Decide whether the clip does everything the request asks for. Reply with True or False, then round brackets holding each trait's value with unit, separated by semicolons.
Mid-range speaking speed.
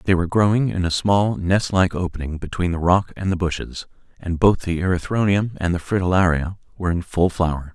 True (195 wpm)